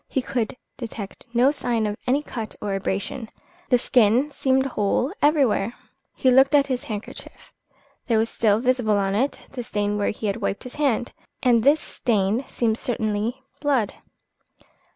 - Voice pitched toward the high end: Yes, high, 235 Hz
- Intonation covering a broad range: No, average, 3.9 semitones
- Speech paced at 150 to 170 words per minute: Yes, average, 160 wpm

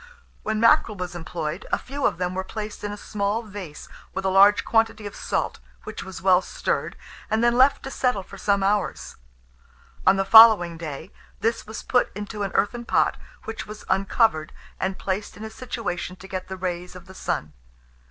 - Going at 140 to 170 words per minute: No, average, 190 wpm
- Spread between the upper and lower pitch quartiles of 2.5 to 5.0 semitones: Yes, average, 3.0 semitones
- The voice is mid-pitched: No, high, 200 Hz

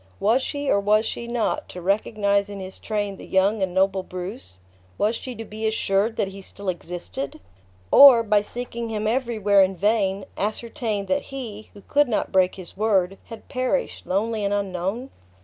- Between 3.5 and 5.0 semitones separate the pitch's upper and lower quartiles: No, average, 2.9 semitones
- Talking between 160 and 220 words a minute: Yes, average, 180 wpm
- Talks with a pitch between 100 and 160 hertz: No, high, 205 Hz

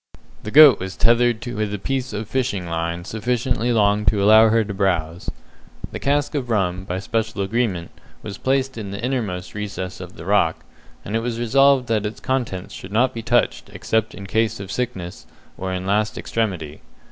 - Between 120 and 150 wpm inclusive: No, average, 185 wpm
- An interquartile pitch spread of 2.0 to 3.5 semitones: No, average, 4.1 semitones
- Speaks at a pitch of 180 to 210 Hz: No, low, 105 Hz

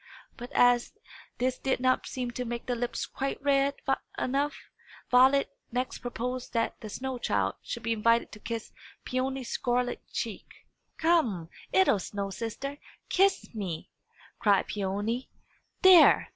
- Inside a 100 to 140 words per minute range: Yes, slow, 135 wpm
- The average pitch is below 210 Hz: No, high, 245 Hz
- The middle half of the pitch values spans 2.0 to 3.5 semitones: Yes, average, 2.7 semitones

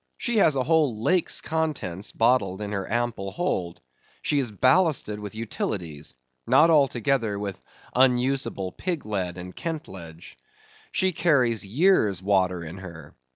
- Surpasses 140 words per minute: No, slow, 135 wpm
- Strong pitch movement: Yes, wide, 7.2 semitones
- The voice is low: Yes, low, 110 Hz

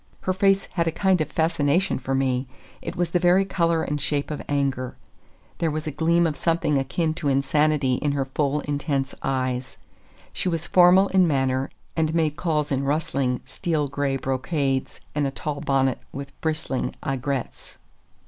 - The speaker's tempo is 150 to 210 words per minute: Yes, average, 170 wpm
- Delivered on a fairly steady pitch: No, average, 3.5 semitones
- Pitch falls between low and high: Yes, medium, 150 Hz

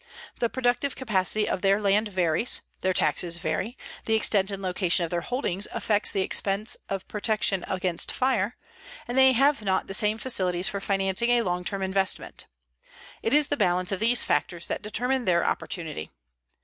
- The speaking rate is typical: Yes, average, 175 wpm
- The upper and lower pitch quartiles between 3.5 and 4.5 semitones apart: Yes, average, 3.9 semitones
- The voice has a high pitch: Yes, high, 195 Hz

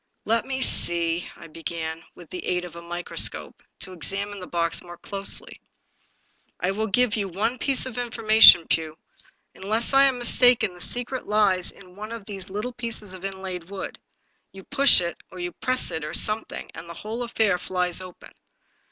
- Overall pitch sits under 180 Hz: No, high, 195 Hz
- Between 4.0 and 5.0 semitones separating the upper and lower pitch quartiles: Yes, average, 4.3 semitones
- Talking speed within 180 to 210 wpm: Yes, average, 185 wpm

